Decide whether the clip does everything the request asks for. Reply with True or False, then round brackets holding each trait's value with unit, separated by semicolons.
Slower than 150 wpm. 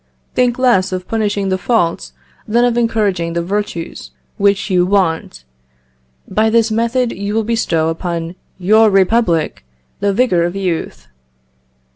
True (135 wpm)